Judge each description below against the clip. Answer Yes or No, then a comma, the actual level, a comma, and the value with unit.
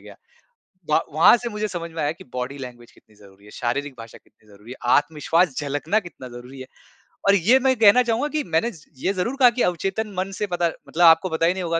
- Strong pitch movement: Yes, wide, 7.3 semitones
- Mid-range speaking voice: Yes, medium, 165 Hz